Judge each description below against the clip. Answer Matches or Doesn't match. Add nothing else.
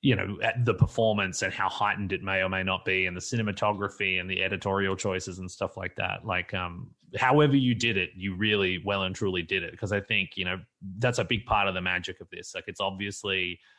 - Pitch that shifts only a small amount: Matches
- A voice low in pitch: Matches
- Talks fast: Matches